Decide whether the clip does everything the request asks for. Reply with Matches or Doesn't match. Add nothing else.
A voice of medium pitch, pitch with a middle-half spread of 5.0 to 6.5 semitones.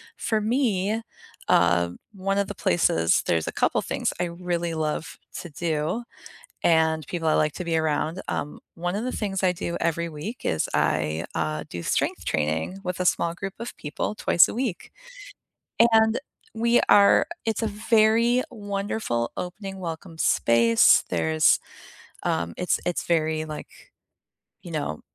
Matches